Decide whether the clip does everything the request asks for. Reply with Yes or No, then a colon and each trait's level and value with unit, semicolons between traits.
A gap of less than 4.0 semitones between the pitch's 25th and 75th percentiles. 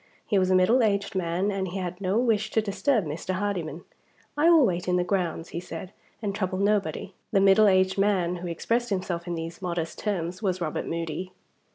Yes: average, 2.8 semitones